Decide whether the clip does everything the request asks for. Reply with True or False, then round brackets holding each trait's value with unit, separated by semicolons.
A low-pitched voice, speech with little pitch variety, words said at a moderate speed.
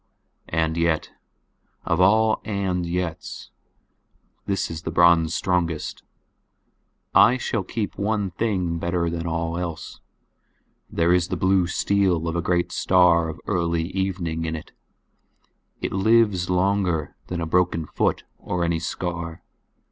False (85 Hz; 2.2 semitones; 125 wpm)